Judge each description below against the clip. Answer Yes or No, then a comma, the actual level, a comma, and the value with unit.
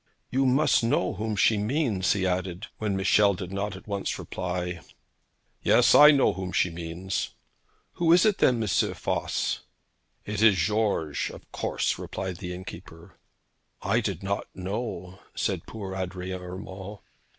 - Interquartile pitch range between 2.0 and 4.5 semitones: Yes, average, 3.2 semitones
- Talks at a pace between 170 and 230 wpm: No, average, 150 wpm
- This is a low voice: Yes, very low, 95 Hz